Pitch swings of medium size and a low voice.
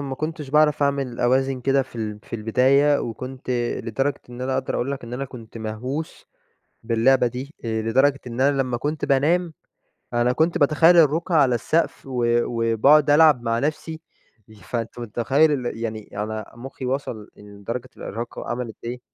Yes: average, 3.6 semitones; low, 130 Hz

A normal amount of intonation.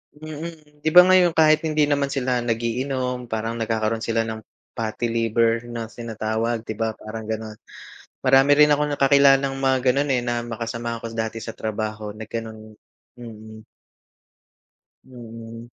Yes: average, 3.4 semitones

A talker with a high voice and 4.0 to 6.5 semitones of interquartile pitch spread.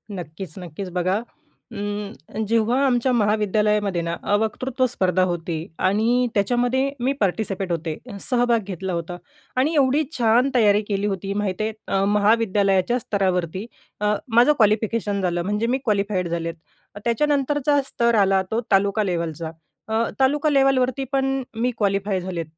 Yes: high, 210 Hz; average, 4.4 semitones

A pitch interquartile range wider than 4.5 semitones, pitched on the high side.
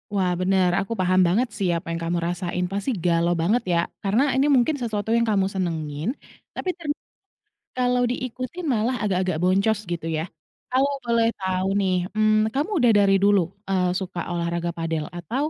Yes: average, 4.9 semitones; high, 195 Hz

